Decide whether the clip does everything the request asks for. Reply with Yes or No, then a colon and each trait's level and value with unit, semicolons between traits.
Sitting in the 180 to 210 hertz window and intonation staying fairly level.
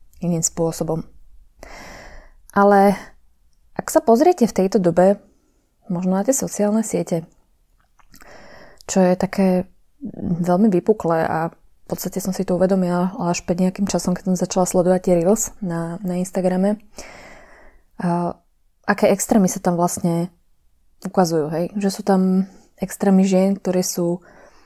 Yes: medium, 185 Hz; narrow, 2.3 semitones